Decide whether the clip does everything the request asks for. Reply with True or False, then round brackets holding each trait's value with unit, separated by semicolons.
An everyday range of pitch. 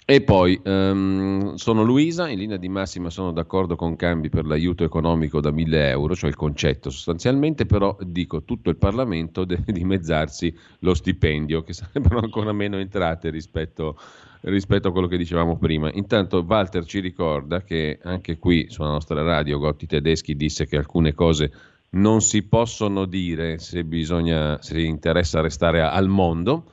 True (3.2 semitones)